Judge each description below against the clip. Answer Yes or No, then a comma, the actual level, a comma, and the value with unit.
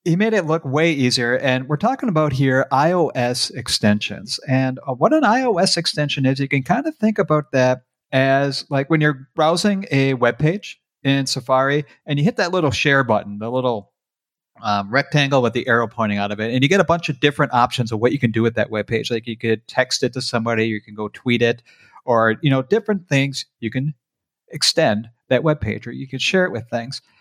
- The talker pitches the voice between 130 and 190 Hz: Yes, low, 135 Hz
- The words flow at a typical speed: No, fast, 225 wpm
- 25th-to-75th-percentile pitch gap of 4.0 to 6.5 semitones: Yes, average, 4.4 semitones